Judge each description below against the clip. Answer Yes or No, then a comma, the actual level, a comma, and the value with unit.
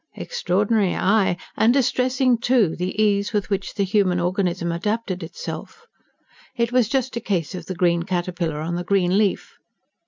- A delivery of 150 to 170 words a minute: Yes, average, 160 wpm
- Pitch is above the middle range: Yes, high, 200 Hz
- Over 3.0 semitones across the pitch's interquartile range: Yes, average, 4.6 semitones